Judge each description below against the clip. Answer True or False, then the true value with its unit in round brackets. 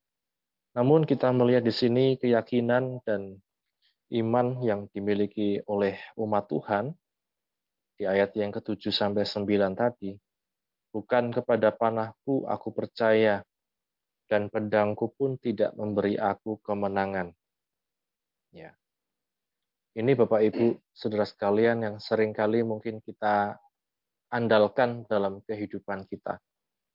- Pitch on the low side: True (110 Hz)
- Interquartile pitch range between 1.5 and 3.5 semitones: True (2.5 semitones)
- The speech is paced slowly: False (100 wpm)